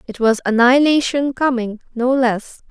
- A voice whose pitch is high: Yes, very high, 250 Hz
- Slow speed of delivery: Yes, slow, 110 wpm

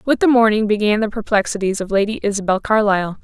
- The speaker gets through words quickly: No, average, 185 wpm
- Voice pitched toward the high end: Yes, high, 210 Hz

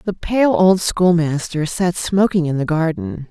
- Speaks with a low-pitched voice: No, medium, 175 Hz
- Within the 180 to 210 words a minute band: No, average, 165 wpm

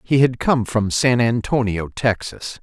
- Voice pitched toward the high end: No, low, 115 Hz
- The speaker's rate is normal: Yes, average, 160 wpm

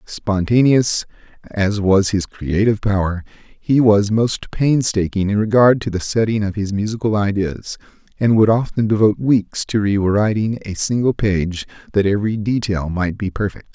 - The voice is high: No, low, 105 Hz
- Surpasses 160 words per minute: No, average, 155 wpm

